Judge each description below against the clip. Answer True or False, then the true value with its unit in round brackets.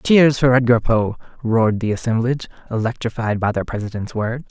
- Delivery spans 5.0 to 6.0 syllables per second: True (5.5 syllables/s)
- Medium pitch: False (115 Hz)